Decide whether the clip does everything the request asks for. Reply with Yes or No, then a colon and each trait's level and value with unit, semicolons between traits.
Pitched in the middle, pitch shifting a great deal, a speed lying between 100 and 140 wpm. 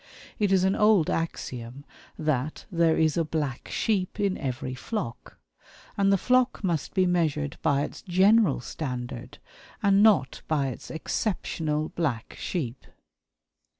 Yes: medium, 160 Hz; wide, 5.8 semitones; slow, 135 wpm